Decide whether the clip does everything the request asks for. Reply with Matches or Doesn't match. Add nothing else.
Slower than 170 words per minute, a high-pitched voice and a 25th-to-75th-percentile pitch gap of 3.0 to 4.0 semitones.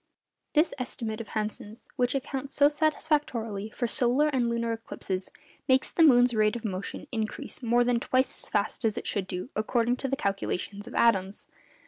Doesn't match